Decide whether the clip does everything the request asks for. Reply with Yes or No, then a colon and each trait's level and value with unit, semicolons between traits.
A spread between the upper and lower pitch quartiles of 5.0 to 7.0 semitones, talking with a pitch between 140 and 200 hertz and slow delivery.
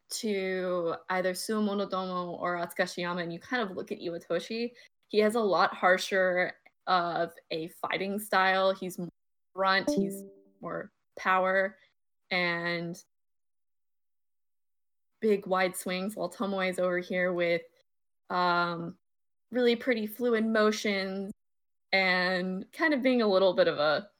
No: average, 2.7 semitones; medium, 185 Hz; slow, 125 wpm